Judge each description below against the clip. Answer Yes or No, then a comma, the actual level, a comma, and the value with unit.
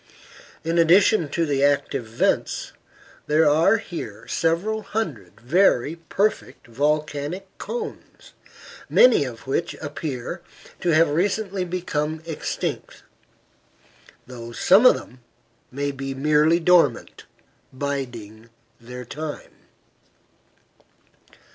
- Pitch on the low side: No, medium, 150 Hz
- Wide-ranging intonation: No, average, 4.4 semitones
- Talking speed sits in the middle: No, slow, 95 wpm